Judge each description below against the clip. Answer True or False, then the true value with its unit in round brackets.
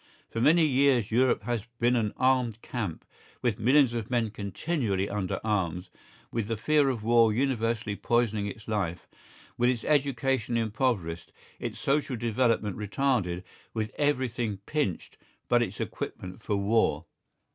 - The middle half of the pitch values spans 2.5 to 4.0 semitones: True (3.7 semitones)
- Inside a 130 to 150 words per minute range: True (140 wpm)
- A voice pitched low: True (115 Hz)